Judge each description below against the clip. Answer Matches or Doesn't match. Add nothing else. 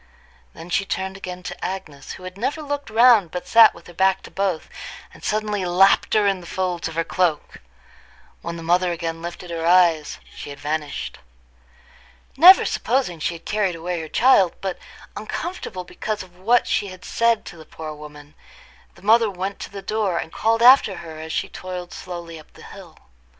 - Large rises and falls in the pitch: Doesn't match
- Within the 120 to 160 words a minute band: Doesn't match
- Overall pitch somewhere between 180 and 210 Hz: Matches